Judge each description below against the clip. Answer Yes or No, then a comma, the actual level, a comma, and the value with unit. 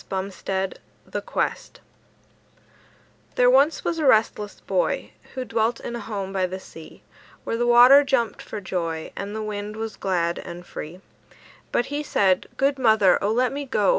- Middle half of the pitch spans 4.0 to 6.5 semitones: Yes, average, 4.7 semitones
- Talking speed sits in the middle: Yes, average, 165 wpm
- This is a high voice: Yes, high, 215 Hz